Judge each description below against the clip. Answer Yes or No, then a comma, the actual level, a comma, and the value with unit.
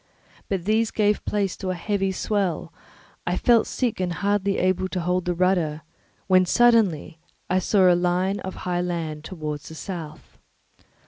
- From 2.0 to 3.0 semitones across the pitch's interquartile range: Yes, narrow, 2.5 semitones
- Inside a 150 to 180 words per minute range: Yes, average, 165 wpm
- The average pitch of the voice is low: No, medium, 185 Hz